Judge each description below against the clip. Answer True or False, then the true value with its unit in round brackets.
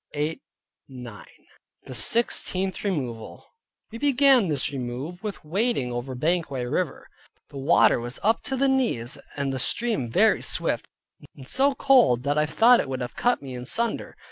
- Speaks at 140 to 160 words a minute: True (155 wpm)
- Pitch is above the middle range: False (150 Hz)